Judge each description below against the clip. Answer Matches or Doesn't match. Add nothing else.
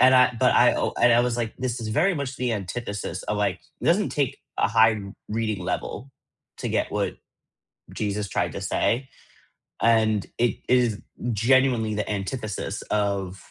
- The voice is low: Matches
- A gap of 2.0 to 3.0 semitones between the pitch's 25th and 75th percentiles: Doesn't match